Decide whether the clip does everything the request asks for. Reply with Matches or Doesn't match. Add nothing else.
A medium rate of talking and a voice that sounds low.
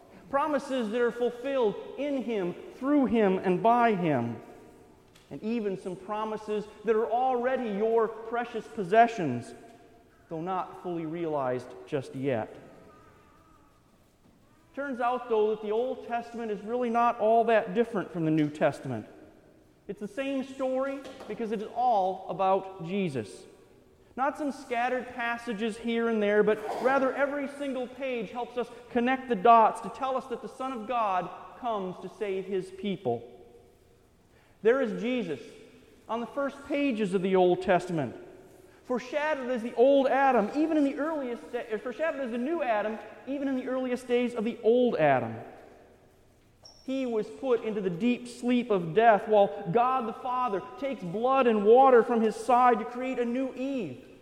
Doesn't match